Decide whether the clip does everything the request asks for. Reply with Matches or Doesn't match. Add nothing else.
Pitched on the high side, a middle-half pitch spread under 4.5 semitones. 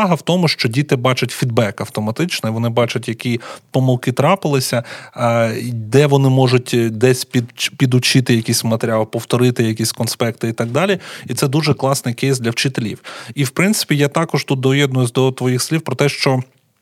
Doesn't match